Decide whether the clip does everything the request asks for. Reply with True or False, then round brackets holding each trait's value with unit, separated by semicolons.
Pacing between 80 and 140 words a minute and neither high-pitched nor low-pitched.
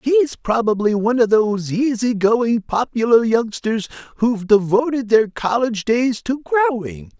False (135 wpm; 230 Hz)